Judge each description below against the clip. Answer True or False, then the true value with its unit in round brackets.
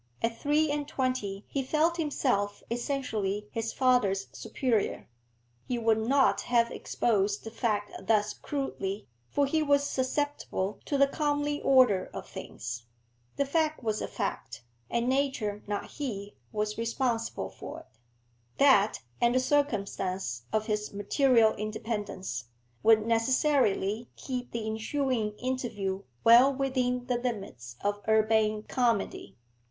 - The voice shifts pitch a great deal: False (4.4 semitones)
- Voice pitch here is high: True (230 Hz)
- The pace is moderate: False (130 wpm)